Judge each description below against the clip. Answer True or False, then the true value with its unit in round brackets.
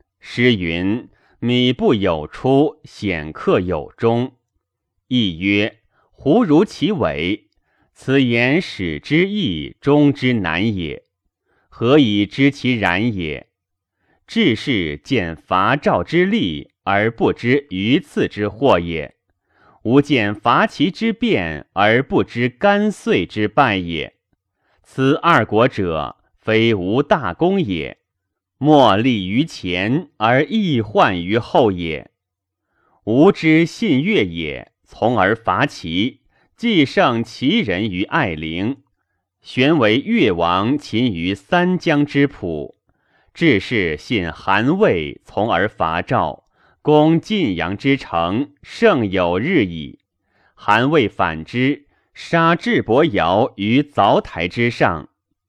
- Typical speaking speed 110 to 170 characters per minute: True (145 characters per minute)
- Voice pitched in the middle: False (120 Hz)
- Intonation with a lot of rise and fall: True (7.4 semitones)